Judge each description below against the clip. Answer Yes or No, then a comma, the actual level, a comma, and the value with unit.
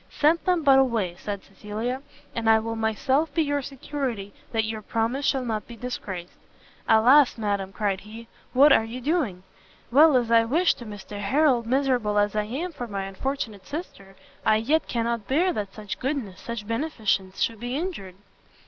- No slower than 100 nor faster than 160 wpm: No, average, 175 wpm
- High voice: Yes, high, 230 Hz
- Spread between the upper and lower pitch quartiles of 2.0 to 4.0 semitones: No, average, 4.7 semitones